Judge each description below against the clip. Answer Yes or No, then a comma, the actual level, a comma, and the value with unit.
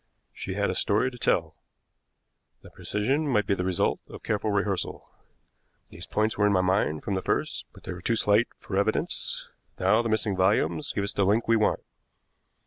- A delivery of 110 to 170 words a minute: No, average, 195 wpm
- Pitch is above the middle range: No, low, 105 Hz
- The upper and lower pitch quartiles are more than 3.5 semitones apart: No, narrow, 2.6 semitones